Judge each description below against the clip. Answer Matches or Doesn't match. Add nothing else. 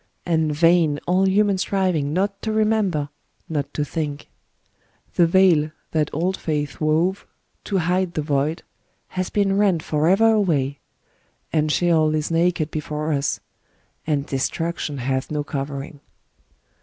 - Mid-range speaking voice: Matches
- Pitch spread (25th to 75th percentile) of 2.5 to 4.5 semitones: Matches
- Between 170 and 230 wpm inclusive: Doesn't match